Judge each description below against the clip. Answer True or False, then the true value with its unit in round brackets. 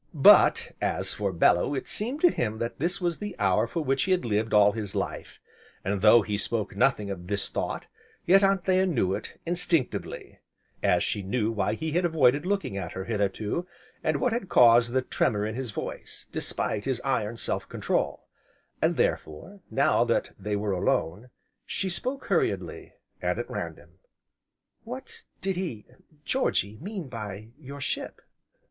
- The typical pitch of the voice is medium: False (120 Hz)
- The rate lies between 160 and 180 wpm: True (165 wpm)